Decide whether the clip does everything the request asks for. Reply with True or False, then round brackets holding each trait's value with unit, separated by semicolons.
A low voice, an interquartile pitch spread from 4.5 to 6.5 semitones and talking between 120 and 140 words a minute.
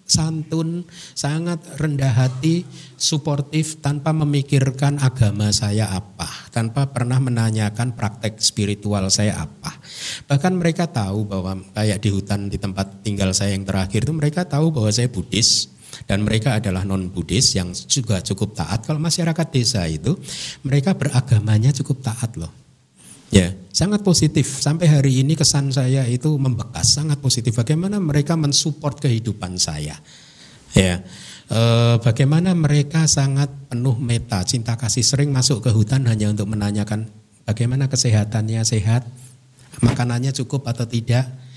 True (125 Hz; 5.2 semitones; 135 wpm)